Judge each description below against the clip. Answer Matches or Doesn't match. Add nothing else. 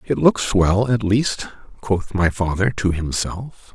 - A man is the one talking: Matches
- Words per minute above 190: Doesn't match